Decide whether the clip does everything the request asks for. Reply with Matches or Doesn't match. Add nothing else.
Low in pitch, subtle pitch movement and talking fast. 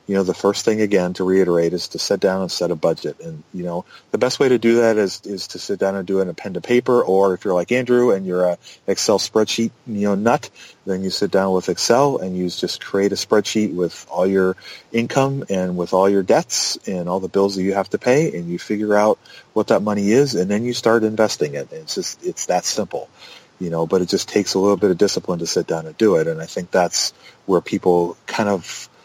Doesn't match